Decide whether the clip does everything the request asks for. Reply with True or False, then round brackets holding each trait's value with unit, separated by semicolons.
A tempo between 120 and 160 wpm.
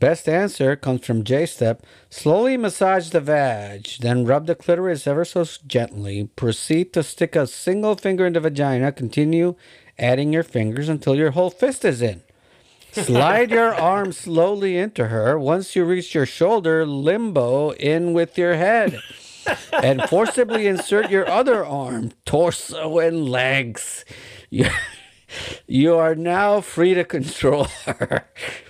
True (140 wpm)